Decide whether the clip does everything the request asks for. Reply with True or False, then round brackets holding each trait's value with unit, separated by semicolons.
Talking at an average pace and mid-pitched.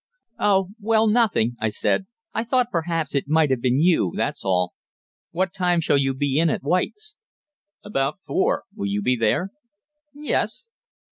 True (160 wpm; 165 Hz)